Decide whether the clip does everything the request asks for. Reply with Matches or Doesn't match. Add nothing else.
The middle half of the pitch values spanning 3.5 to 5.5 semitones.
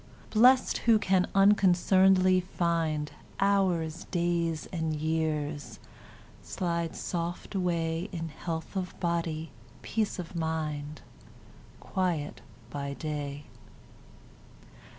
Doesn't match